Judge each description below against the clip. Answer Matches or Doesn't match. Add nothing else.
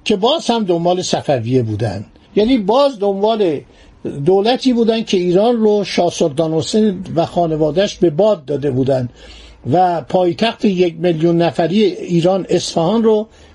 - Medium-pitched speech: Matches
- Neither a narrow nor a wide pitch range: Matches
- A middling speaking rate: Matches